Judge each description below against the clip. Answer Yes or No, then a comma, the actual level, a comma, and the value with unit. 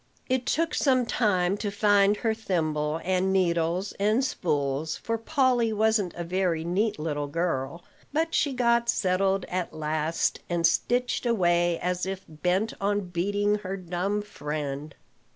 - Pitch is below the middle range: No, medium, 185 Hz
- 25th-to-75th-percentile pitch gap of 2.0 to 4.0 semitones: No, average, 4.5 semitones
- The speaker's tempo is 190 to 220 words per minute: No, average, 145 wpm